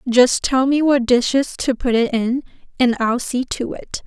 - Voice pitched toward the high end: Yes, very high, 250 Hz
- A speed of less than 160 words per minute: No, fast, 205 wpm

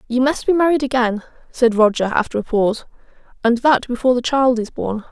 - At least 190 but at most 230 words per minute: Yes, average, 200 wpm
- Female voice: Yes, female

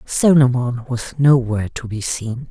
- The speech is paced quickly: No, average, 145 wpm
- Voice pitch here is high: No, low, 125 Hz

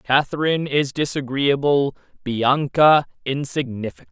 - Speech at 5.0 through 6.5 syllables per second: No, 4.4 syllables/s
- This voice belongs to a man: Yes, male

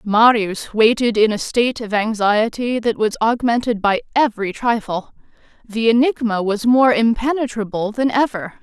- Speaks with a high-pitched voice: Yes, high, 225 Hz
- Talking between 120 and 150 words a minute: Yes, average, 140 wpm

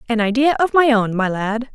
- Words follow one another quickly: Yes, fast, 240 wpm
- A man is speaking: No, female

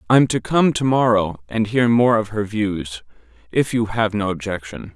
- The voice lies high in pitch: No, low, 110 Hz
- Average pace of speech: Yes, average, 180 wpm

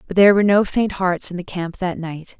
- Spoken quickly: Yes, fast, 275 wpm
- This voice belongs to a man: No, female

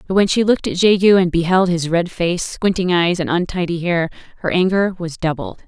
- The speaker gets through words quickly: Yes, fast, 210 wpm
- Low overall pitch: No, medium, 175 Hz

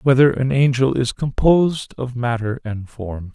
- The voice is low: Yes, low, 125 Hz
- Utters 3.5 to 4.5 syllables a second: Yes, 4.4 syllables/s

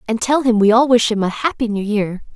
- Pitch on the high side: Yes, high, 225 Hz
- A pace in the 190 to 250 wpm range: No, fast, 280 wpm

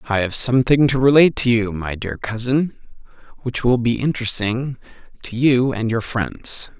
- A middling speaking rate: Yes, average, 170 wpm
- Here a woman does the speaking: No, male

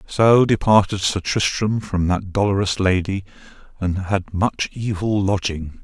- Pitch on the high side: No, low, 100 Hz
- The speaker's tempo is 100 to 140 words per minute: Yes, slow, 135 wpm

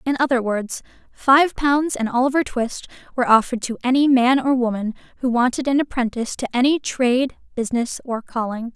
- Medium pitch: No, very high, 250 Hz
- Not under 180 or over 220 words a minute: No, average, 170 wpm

